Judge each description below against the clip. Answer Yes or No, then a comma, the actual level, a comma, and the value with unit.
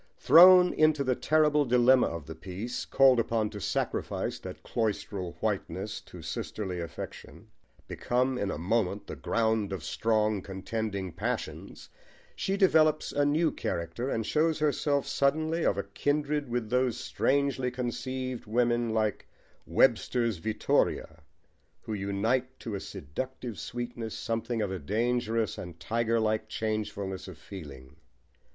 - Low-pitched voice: Yes, low, 115 Hz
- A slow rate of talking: Yes, slow, 130 wpm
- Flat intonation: No, average, 4.6 semitones